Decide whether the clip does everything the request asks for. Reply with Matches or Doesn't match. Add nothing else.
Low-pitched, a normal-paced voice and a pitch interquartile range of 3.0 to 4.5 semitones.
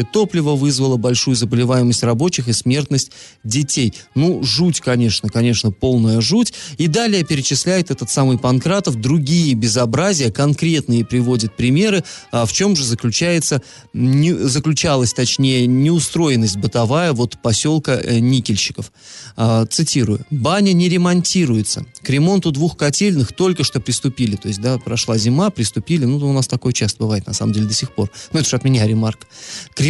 Doesn't match